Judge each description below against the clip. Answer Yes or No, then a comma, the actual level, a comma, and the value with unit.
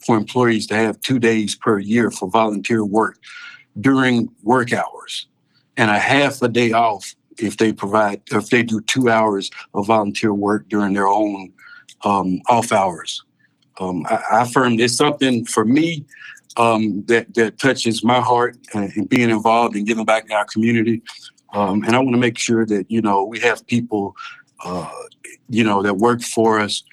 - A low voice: Yes, low, 115 Hz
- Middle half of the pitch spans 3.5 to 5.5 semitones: No, narrow, 2.4 semitones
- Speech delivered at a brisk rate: No, average, 180 wpm